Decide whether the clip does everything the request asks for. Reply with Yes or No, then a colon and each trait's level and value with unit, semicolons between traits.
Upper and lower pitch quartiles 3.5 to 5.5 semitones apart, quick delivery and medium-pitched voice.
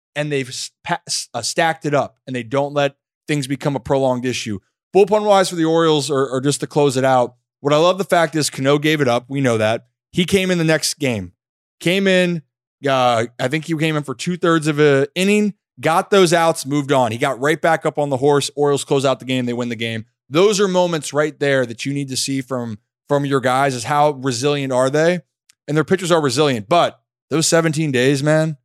Yes: average, 3.8 semitones; fast, 230 wpm; medium, 145 Hz